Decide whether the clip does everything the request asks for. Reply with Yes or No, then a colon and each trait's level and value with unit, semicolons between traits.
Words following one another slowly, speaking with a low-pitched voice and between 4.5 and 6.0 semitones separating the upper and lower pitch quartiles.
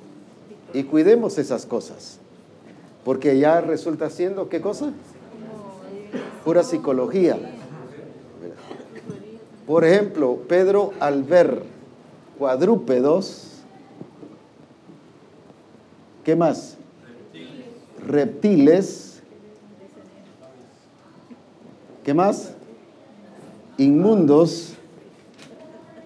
No: slow, 55 wpm; medium, 170 Hz; average, 4.8 semitones